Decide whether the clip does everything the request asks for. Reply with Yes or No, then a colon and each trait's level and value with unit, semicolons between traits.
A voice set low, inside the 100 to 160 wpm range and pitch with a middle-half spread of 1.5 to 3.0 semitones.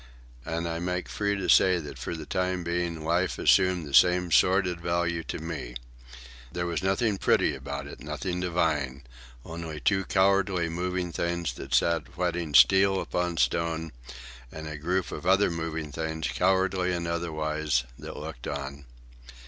Yes: very low, 85 Hz; average, 155 wpm; average, 2.7 semitones